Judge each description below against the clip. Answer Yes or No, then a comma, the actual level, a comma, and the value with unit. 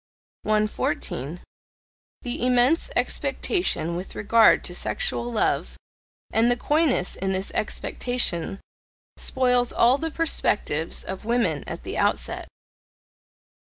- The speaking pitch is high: Yes, high, 235 Hz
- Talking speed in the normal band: No, slow, 105 wpm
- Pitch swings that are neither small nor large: Yes, average, 4.7 semitones